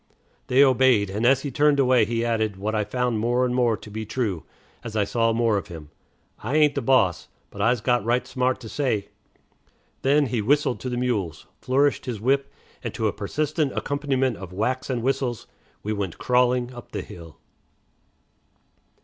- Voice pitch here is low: Yes, low, 120 Hz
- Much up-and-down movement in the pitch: No, average, 3.4 semitones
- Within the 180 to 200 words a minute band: Yes, average, 185 wpm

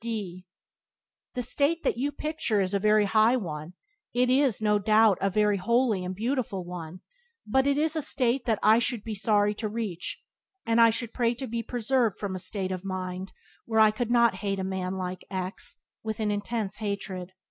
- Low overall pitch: No, high, 215 Hz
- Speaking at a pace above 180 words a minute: Yes, fast, 205 wpm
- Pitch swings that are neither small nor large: Yes, average, 3.8 semitones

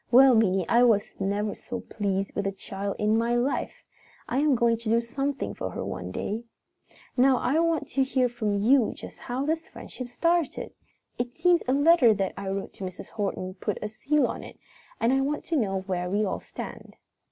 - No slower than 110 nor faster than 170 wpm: No, fast, 205 wpm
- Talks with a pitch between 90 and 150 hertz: No, high, 235 Hz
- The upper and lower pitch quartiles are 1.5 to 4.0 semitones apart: No, average, 5.0 semitones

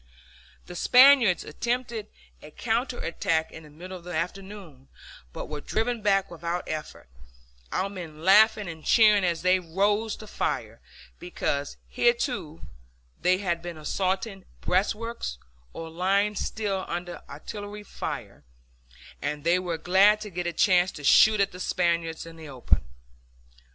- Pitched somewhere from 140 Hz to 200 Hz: Yes, medium, 185 Hz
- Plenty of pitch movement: No, average, 4.0 semitones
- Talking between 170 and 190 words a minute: No, average, 145 wpm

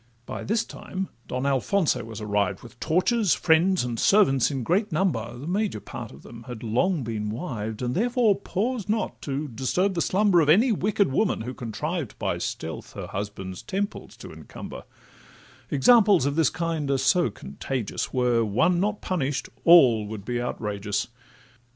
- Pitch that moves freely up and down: Yes, wide, 8.5 semitones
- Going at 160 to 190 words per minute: Yes, average, 165 wpm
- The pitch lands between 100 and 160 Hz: Yes, medium, 140 Hz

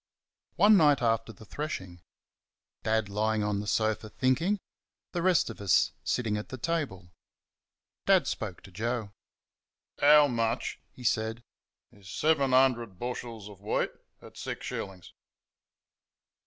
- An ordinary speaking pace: No, slow, 130 wpm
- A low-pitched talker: Yes, low, 115 Hz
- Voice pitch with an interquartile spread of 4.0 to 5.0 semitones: Yes, average, 4.4 semitones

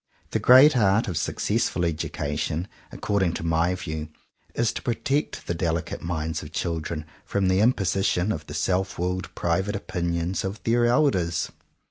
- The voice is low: Yes, very low, 90 Hz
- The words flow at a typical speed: Yes, average, 150 wpm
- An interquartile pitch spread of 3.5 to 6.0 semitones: Yes, average, 3.9 semitones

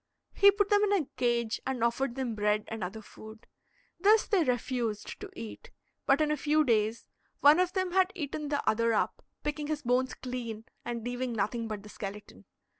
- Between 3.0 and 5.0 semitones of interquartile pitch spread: No, wide, 5.5 semitones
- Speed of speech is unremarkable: Yes, average, 190 wpm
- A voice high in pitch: Yes, very high, 250 Hz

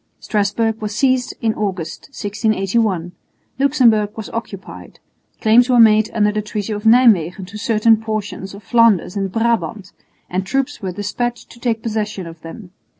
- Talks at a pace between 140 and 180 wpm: Yes, average, 150 wpm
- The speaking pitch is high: Yes, high, 215 Hz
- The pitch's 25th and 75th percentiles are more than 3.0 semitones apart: No, average, 2.7 semitones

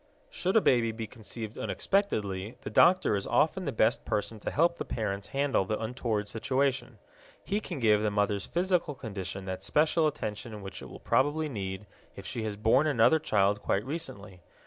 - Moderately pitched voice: No, low, 115 Hz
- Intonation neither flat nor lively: No, wide, 6.1 semitones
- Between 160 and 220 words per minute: Yes, average, 180 wpm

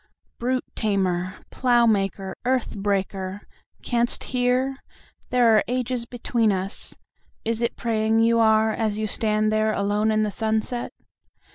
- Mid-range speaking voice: No, high, 220 Hz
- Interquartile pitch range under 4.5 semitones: Yes, narrow, 2.5 semitones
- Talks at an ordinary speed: No, slow, 125 wpm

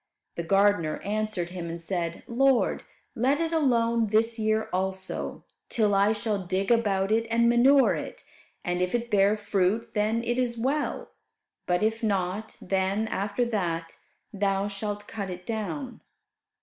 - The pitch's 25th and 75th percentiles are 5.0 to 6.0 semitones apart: No, average, 3.4 semitones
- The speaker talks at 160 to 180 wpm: No, average, 150 wpm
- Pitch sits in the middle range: No, high, 210 Hz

